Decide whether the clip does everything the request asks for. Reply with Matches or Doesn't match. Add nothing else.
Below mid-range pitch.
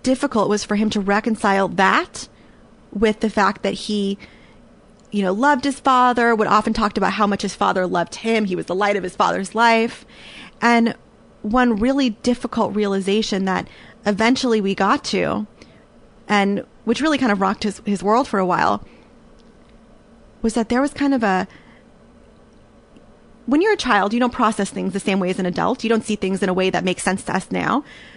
Doesn't match